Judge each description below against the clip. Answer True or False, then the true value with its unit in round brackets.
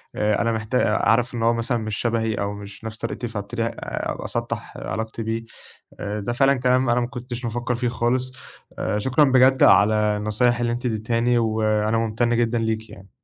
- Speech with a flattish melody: True (1.9 semitones)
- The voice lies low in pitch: True (115 Hz)